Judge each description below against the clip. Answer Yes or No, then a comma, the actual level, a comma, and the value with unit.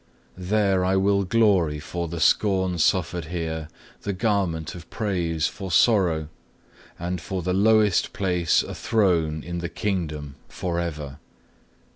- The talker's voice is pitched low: Yes, very low, 90 Hz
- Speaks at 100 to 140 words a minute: Yes, slow, 135 wpm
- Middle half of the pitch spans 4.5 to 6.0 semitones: No, average, 3.2 semitones